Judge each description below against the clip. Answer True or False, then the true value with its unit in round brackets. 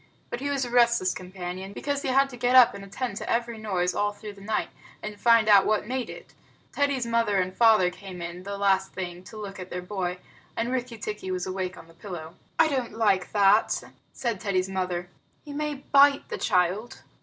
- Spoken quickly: True (210 wpm)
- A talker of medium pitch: False (205 Hz)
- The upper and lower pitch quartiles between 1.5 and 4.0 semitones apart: False (4.4 semitones)